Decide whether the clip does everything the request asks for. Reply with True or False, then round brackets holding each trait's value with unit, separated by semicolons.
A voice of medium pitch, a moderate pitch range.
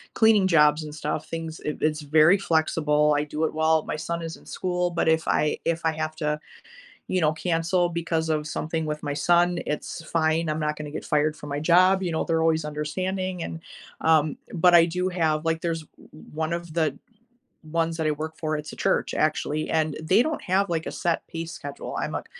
False (160 Hz; 1.8 semitones)